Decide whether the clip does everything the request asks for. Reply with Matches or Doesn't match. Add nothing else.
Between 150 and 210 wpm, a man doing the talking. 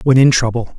Doesn't match